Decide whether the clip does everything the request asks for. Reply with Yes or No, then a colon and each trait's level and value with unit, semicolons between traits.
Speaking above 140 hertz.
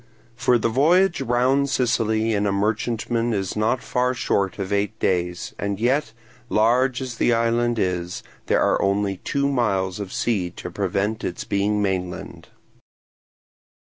No: low, 110 Hz